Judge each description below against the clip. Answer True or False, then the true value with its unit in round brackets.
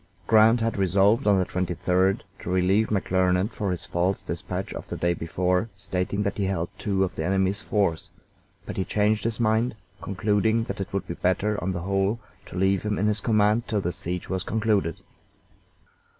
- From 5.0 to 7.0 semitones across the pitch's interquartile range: False (2.6 semitones)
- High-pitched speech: False (95 Hz)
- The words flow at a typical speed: True (190 wpm)